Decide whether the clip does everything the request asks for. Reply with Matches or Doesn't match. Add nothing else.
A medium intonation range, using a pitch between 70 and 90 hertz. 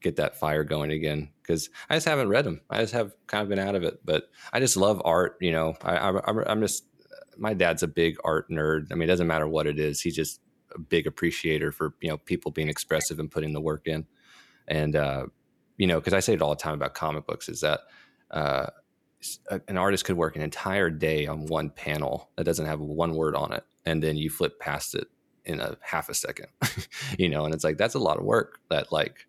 Doesn't match